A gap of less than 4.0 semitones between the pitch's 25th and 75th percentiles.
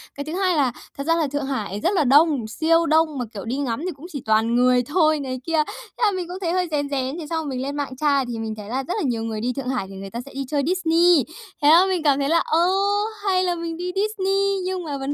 No: average, 4.8 semitones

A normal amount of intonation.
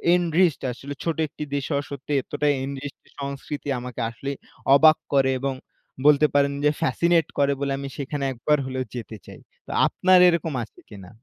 No: narrow, 2.0 semitones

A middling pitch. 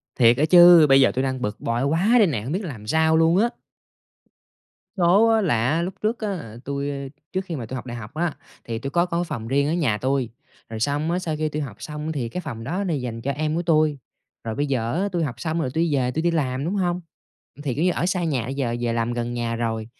Yes: medium, 145 Hz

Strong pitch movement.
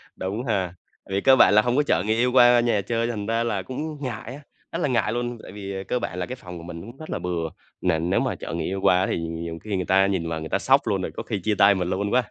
No: average, 4.8 semitones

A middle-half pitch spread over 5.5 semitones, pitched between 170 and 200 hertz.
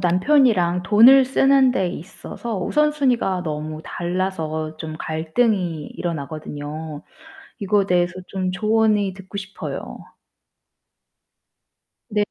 No: average, 5.2 semitones; medium, 185 Hz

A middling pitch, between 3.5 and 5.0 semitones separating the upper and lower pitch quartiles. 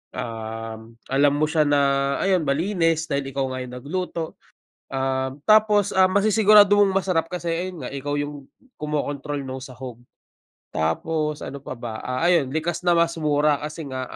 Yes: medium, 145 Hz; average, 4.4 semitones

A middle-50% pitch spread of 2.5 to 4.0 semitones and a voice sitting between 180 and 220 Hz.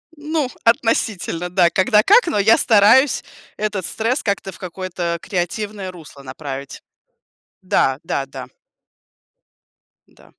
No: average, 4.6 semitones; high, 190 Hz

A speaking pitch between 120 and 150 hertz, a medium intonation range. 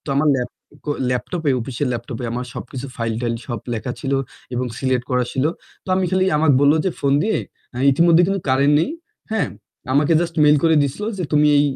Yes: medium, 140 Hz; average, 4.5 semitones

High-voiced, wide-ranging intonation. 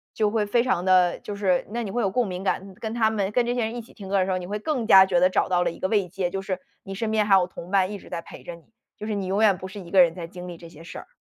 No: high, 195 Hz; average, 2.9 semitones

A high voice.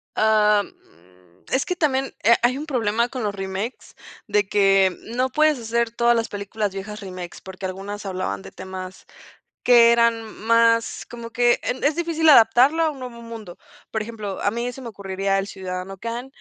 Yes: high, 225 Hz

